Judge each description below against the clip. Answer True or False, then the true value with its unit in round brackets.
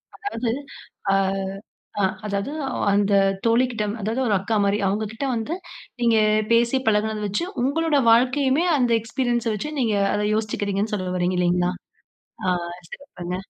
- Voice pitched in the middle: False (220 Hz)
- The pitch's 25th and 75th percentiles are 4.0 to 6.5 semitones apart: False (3.5 semitones)